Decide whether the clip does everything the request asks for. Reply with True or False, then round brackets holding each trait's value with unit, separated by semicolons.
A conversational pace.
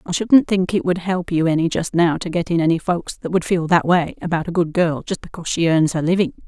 False (280 wpm)